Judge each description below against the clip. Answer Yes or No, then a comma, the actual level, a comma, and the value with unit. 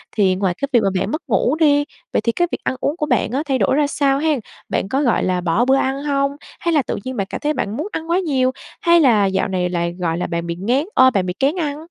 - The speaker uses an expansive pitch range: Yes, wide, 7.1 semitones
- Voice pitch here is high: Yes, very high, 260 Hz